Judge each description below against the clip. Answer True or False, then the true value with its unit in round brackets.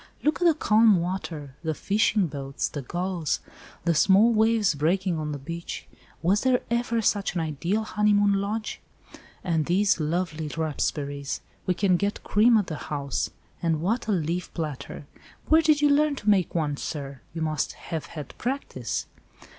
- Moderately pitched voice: True (180 Hz)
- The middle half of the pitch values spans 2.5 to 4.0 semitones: False (5.5 semitones)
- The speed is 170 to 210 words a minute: False (160 wpm)